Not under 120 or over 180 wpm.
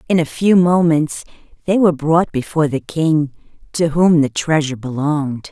Yes: average, 165 wpm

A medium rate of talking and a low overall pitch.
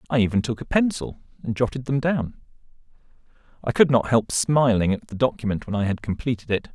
Yes: average, 195 wpm; low, 120 Hz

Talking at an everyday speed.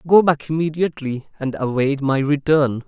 Yes: average, 145 wpm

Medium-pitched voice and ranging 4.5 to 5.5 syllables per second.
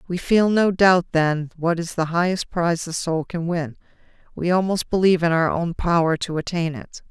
Yes: medium, 170 Hz; 5.1 syllables/s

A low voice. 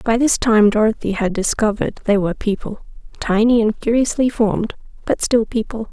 No: high, 220 Hz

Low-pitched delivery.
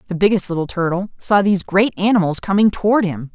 No: high, 190 Hz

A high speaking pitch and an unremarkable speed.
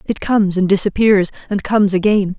Yes: high, 195 Hz; average, 175 wpm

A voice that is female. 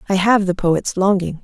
Yes: female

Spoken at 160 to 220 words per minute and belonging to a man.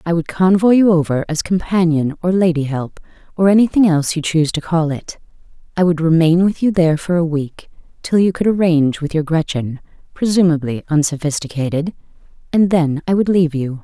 No: average, 180 wpm; female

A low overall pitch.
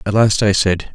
Yes: low, 100 Hz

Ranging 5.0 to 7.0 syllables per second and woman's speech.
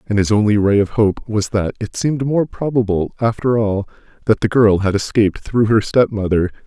No: 5.2 syllables/s; male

